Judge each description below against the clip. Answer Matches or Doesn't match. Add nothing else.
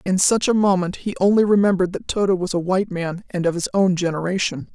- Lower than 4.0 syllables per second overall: Doesn't match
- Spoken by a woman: Matches